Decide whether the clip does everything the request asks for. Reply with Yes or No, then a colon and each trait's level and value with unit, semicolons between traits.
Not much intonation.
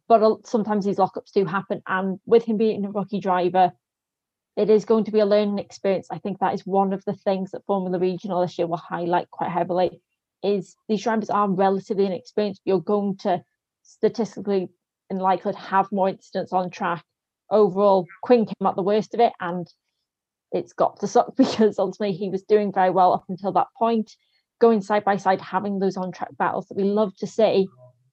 Yes: narrow, 2.2 semitones